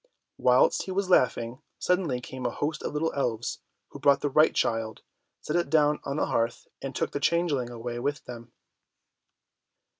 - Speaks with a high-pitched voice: No, medium, 140 Hz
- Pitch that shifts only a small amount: No, average, 4.7 semitones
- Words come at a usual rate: Yes, average, 175 wpm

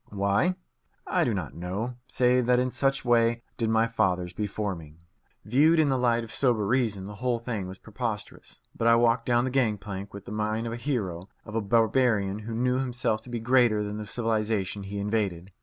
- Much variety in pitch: No, average, 3.3 semitones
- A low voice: Yes, low, 110 Hz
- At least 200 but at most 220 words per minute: Yes, fast, 205 wpm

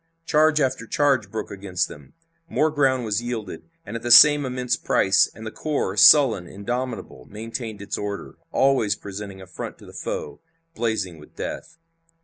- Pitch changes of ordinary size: Yes, average, 4.6 semitones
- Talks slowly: No, average, 165 wpm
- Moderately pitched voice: No, low, 115 Hz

